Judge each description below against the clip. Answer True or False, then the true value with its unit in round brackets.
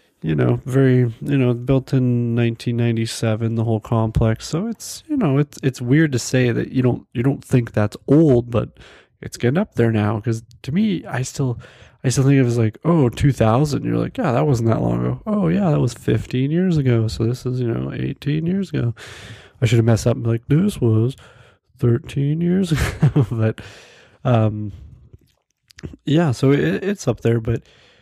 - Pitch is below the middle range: True (125 Hz)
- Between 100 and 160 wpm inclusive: False (205 wpm)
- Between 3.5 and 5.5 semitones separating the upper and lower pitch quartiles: True (3.8 semitones)